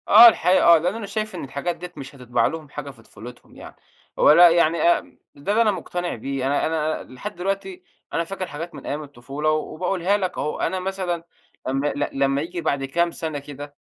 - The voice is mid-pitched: Yes, medium, 160 Hz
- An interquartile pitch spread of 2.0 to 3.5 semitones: No, average, 4.2 semitones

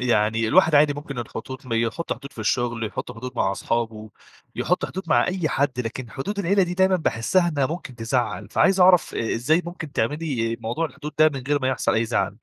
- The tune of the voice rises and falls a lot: Yes, wide, 6.2 semitones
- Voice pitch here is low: Yes, low, 130 Hz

